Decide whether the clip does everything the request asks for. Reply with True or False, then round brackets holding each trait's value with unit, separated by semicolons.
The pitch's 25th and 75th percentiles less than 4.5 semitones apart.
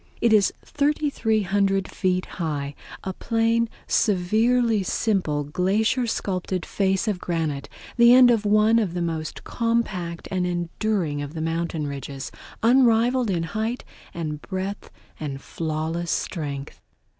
False (5.4 semitones)